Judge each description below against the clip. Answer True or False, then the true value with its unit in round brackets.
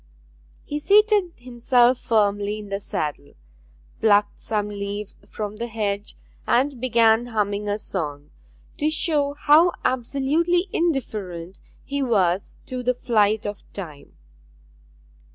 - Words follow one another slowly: True (115 wpm)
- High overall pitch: True (225 Hz)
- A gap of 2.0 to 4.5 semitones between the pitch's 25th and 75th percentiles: False (5.1 semitones)